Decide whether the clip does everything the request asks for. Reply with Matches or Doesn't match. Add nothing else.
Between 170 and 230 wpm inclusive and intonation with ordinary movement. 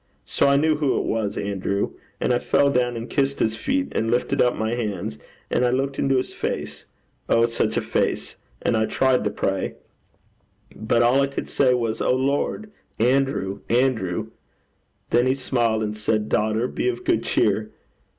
Matches